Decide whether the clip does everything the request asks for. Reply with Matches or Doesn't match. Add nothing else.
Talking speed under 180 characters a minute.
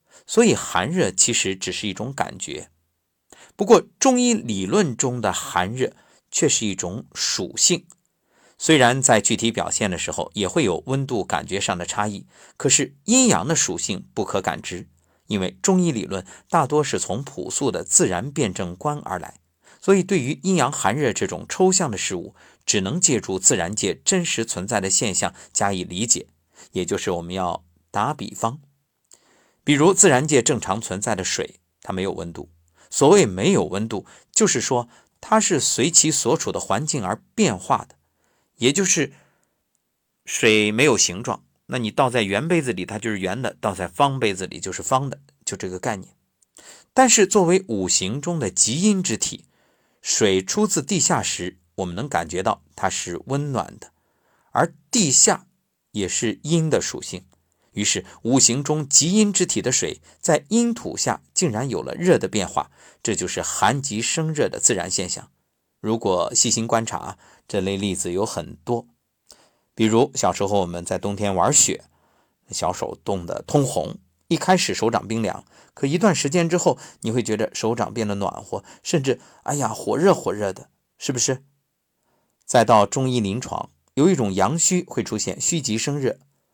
Doesn't match